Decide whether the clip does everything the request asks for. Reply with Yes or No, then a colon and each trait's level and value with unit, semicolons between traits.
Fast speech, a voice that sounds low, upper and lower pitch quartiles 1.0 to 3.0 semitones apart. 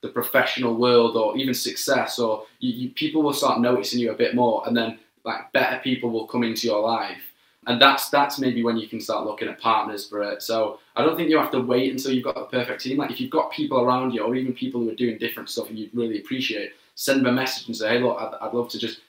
Yes: fast, 275 wpm; low, 125 Hz; average, 2.7 semitones